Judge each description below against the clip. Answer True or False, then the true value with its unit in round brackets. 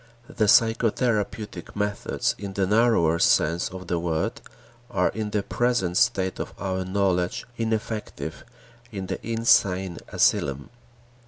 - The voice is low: True (100 Hz)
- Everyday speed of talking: False (120 wpm)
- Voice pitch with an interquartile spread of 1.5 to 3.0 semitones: False (3.4 semitones)